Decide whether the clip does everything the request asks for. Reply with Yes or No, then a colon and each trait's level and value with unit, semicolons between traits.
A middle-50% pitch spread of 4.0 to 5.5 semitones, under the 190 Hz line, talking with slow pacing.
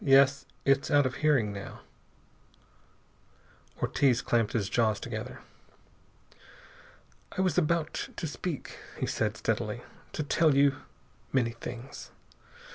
Yes: average, 4.3 semitones; low, 135 Hz; slow, 115 wpm